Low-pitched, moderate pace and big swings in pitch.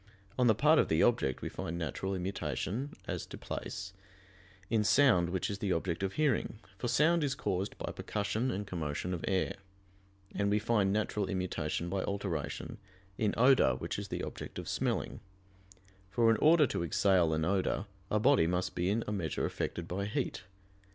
No: low, 100 Hz; average, 180 wpm; average, 4.3 semitones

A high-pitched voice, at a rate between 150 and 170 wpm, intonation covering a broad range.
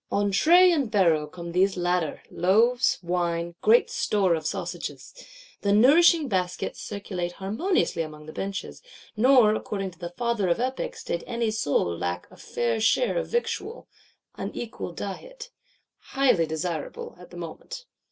Yes: high, 200 Hz; average, 155 wpm; wide, 6.1 semitones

